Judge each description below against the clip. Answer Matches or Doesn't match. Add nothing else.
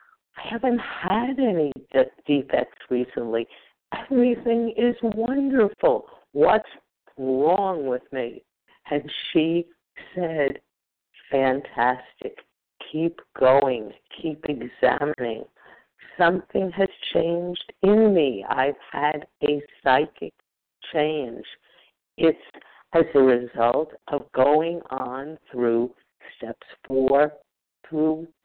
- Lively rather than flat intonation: Matches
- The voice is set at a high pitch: Doesn't match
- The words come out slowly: Matches